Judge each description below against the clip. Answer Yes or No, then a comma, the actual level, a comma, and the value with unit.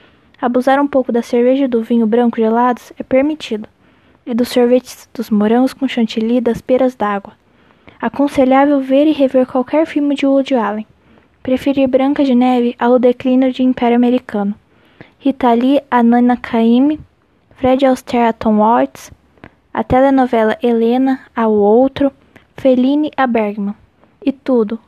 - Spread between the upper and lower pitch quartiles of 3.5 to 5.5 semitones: No, narrow, 2.4 semitones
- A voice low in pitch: No, very high, 255 Hz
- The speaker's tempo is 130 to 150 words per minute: Yes, average, 140 wpm